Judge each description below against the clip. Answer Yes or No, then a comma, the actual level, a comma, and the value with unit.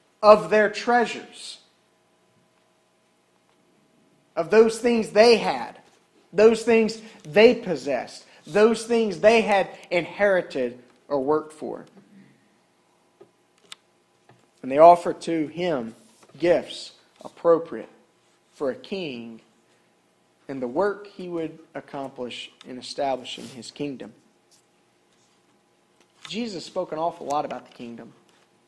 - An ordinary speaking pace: No, slow, 100 wpm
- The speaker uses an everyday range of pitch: No, wide, 7.5 semitones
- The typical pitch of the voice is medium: Yes, medium, 170 Hz